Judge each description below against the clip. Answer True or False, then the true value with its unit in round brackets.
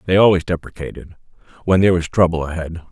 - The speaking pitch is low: True (85 Hz)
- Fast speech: False (165 wpm)